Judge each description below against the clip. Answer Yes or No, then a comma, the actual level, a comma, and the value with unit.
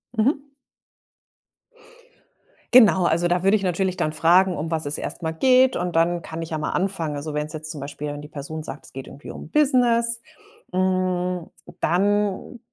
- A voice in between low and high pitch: Yes, medium, 175 Hz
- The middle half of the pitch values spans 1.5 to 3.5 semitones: No, average, 4.1 semitones